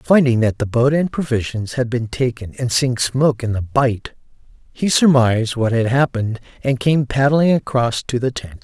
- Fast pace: No, average, 190 wpm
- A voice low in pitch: Yes, low, 125 Hz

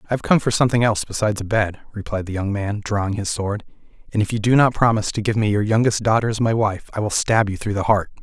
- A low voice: Yes, low, 105 Hz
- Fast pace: Yes, fast, 275 wpm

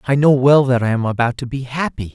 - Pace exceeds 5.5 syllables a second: Yes, 6.0 syllables/s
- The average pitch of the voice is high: No, low, 130 Hz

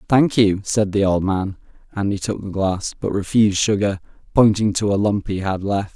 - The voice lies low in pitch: Yes, low, 100 Hz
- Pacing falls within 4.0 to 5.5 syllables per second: Yes, 5.0 syllables/s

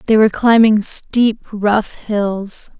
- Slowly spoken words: Yes, slow, 130 wpm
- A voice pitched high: Yes, high, 215 Hz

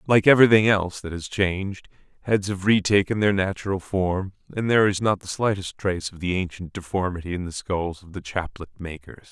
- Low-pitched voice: Yes, very low, 95 Hz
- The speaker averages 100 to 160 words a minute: No, average, 200 wpm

